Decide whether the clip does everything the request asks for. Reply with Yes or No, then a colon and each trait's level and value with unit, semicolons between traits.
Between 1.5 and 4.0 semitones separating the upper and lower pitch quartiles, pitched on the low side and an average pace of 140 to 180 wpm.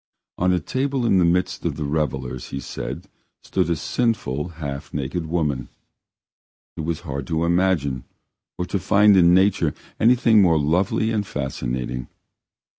No: wide, 5.4 semitones; very low, 85 Hz; average, 150 wpm